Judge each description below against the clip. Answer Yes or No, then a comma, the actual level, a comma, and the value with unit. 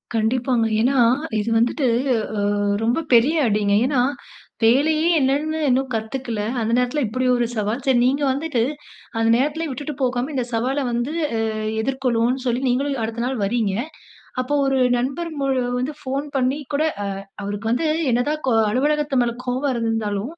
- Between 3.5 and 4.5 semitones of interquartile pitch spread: No, average, 3.0 semitones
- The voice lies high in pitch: Yes, very high, 255 Hz